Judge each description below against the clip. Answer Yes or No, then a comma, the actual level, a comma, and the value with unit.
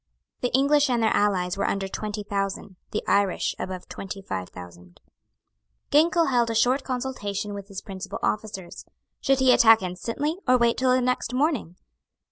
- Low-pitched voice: No, high, 215 Hz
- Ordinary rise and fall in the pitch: Yes, average, 4.7 semitones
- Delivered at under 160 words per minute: No, average, 165 wpm